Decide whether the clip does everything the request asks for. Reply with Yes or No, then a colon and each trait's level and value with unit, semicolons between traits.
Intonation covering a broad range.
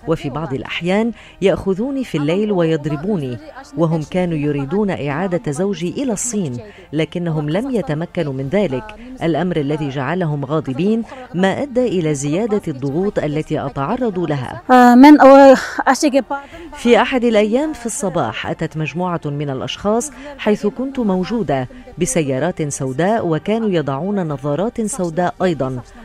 Yes: wide, 6.7 semitones